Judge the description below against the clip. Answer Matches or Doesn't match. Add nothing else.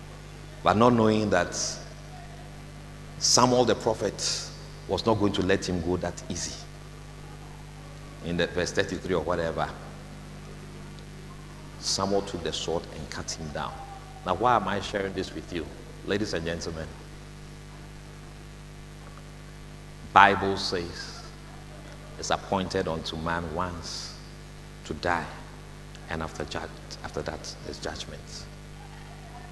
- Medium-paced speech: Doesn't match